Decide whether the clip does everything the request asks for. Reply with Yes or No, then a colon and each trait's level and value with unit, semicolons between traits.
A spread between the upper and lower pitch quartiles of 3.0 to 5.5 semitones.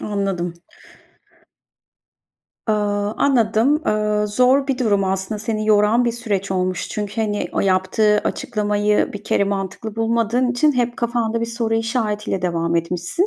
No: narrow, 2.6 semitones